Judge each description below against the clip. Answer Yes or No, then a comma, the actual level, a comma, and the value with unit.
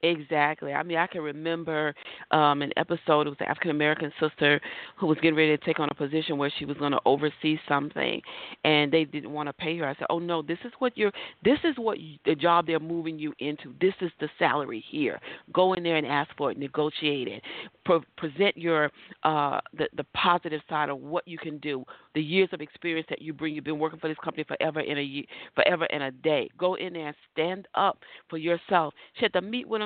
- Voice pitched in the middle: Yes, medium, 160 Hz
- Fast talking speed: Yes, fast, 235 wpm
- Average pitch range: No, narrow, 2.3 semitones